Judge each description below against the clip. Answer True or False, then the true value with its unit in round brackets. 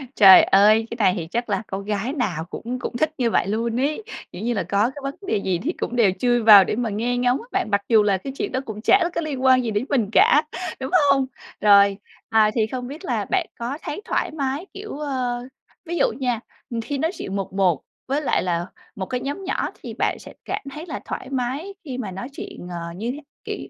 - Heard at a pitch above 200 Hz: True (240 Hz)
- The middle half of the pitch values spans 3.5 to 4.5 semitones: False (5.1 semitones)